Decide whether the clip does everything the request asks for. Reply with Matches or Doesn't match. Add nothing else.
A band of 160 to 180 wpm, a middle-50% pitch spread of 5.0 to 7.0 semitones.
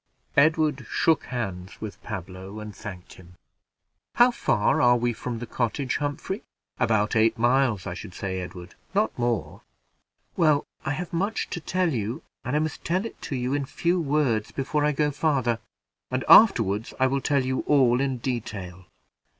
Matches